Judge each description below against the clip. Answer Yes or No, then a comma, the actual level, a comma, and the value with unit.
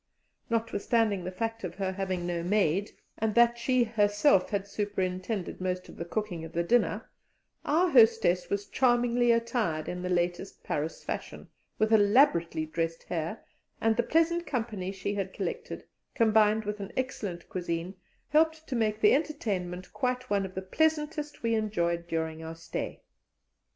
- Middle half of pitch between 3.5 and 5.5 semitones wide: Yes, average, 4.7 semitones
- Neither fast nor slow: Yes, average, 155 wpm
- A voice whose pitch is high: Yes, high, 205 Hz